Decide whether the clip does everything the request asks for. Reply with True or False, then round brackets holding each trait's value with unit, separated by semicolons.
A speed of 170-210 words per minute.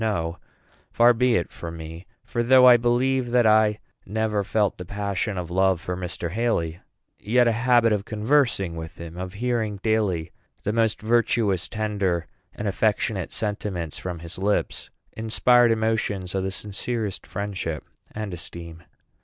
False (155 wpm)